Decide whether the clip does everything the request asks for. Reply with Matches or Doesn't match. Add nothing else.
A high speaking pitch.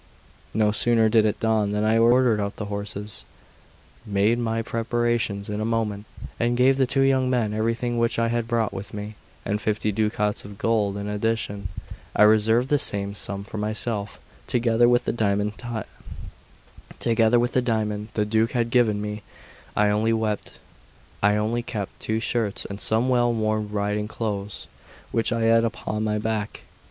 Doesn't match